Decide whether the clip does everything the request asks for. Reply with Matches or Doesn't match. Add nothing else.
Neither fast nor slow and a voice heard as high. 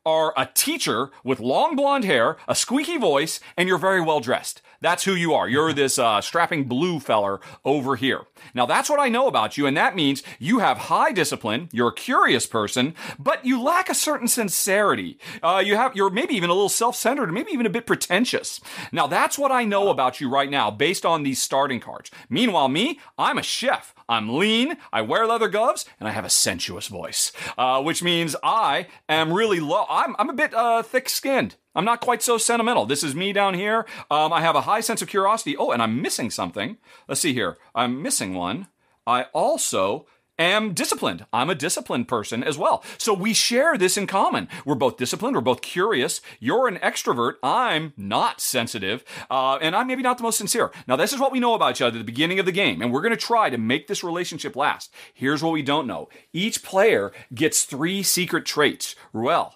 Doesn't match